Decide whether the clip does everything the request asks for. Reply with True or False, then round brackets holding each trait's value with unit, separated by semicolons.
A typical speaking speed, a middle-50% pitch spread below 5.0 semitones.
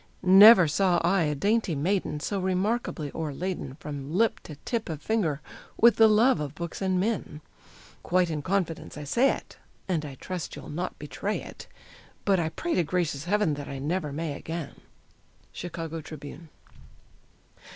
True (160 wpm; 4.6 semitones)